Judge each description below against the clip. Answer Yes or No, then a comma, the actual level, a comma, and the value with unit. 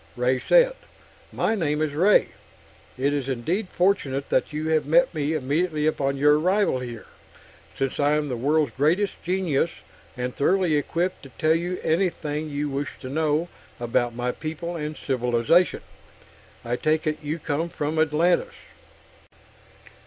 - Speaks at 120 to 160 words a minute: Yes, average, 150 wpm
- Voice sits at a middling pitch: Yes, medium, 150 Hz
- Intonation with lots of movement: No, average, 3.5 semitones